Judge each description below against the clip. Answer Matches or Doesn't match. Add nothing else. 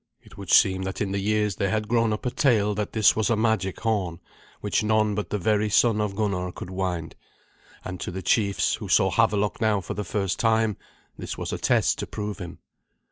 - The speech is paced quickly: Matches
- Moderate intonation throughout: Doesn't match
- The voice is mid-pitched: Doesn't match